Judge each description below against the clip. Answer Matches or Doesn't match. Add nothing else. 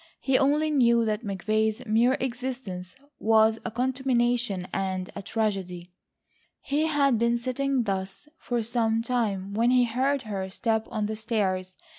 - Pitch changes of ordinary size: Matches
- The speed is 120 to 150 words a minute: Matches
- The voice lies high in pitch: Matches